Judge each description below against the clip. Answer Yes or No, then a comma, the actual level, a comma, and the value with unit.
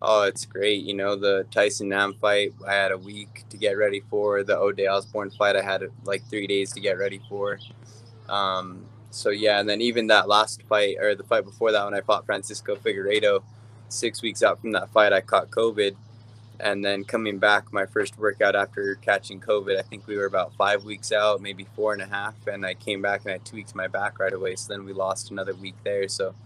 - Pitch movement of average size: No, narrow, 2.0 semitones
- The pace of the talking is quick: Yes, fast, 230 wpm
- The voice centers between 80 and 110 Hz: Yes, low, 105 Hz